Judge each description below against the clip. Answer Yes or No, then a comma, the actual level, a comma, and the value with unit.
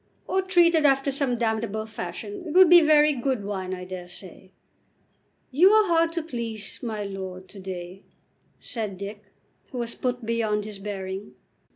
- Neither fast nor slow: Yes, average, 170 wpm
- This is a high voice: Yes, high, 225 Hz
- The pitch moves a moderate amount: No, wide, 7.2 semitones